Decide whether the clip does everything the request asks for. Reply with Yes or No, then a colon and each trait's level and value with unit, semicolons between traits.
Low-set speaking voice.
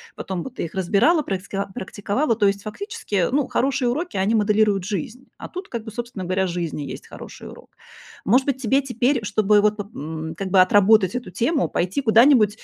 No: high, 215 Hz